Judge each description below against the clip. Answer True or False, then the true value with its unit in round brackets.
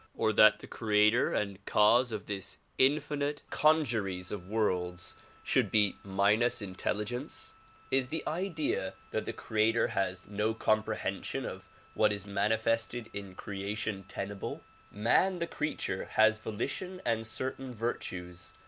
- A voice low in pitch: True (110 Hz)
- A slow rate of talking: True (130 wpm)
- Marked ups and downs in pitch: False (3.5 semitones)